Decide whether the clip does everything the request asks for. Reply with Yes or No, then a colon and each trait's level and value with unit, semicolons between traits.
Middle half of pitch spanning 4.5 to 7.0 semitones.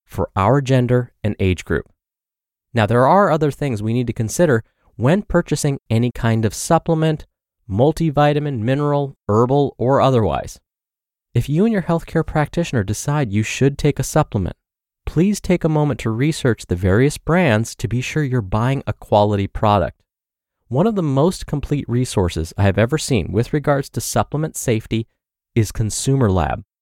Yes: wide, 5.5 semitones